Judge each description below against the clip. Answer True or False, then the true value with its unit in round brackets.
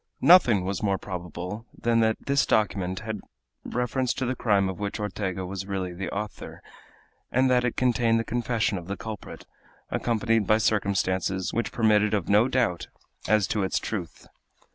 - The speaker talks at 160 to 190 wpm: True (165 wpm)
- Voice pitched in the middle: False (105 Hz)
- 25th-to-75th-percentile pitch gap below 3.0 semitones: False (3.3 semitones)